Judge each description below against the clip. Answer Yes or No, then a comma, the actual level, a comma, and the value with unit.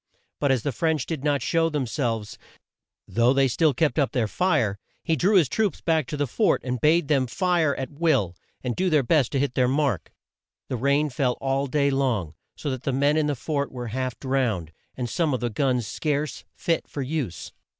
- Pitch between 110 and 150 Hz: Yes, medium, 140 Hz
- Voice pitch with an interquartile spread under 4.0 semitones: Yes, average, 3.5 semitones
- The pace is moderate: No, fast, 210 wpm